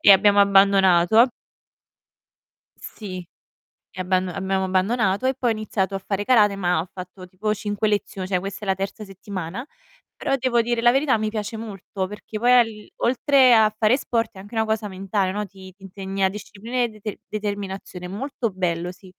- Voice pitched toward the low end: No, high, 200 Hz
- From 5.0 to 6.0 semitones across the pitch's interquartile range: No, average, 2.7 semitones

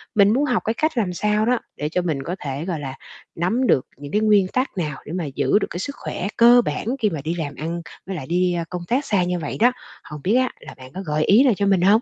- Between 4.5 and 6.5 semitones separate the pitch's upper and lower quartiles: Yes, wide, 5.6 semitones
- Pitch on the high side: No, medium, 180 Hz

